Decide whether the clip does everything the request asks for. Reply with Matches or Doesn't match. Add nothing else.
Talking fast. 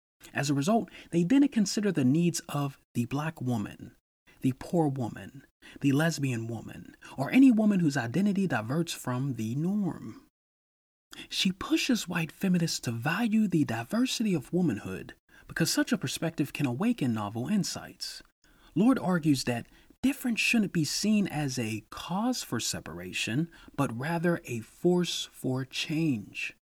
Doesn't match